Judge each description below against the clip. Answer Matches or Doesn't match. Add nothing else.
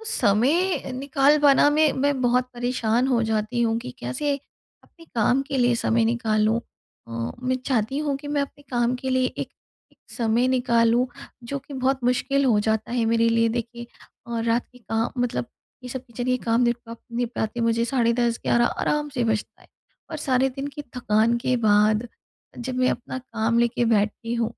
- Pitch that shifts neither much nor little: Doesn't match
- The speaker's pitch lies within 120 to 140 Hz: Doesn't match